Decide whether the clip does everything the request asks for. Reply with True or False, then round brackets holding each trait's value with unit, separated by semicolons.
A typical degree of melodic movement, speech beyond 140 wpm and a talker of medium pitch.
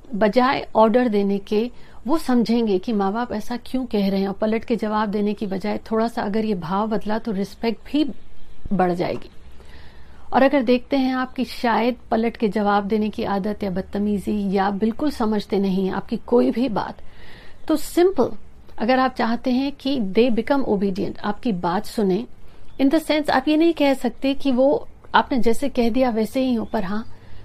False (3.8 semitones; 185 wpm; 225 Hz)